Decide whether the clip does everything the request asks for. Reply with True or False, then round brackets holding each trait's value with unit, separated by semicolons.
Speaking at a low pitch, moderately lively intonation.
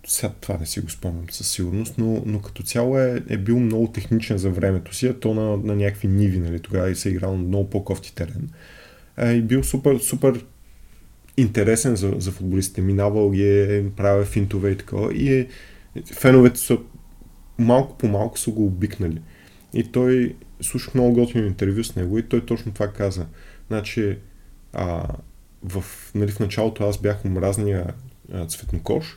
True (105 Hz; 3.3 semitones)